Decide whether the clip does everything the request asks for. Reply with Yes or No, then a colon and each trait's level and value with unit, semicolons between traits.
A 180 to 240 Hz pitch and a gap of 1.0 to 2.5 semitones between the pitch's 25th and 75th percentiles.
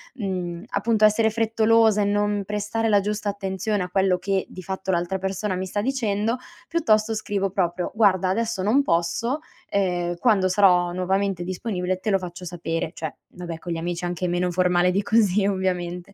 No: high, 190 Hz; average, 2.9 semitones